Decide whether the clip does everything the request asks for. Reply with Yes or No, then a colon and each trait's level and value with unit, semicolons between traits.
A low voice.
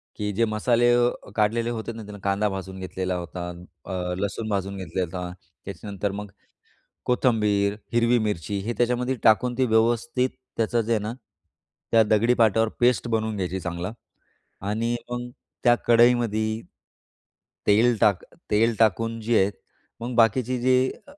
Yes: low, 110 Hz